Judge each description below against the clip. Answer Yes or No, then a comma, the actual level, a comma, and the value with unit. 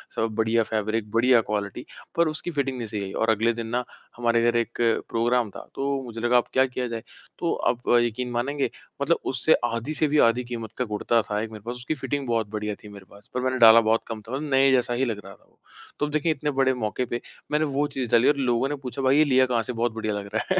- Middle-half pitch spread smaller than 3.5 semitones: Yes, average, 2.9 semitones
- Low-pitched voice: Yes, low, 120 Hz